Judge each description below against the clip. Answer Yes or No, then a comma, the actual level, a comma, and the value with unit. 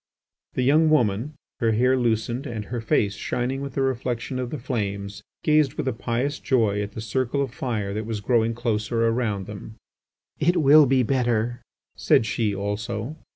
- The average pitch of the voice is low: Yes, low, 120 Hz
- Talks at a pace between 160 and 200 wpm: Yes, average, 175 wpm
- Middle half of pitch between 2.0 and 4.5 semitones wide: Yes, average, 3.4 semitones